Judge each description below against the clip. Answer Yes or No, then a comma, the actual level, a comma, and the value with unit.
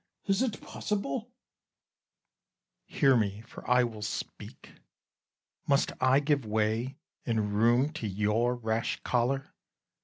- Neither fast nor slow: No, slow, 120 wpm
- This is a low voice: Yes, low, 120 Hz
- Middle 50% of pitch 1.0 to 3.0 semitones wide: No, average, 3.9 semitones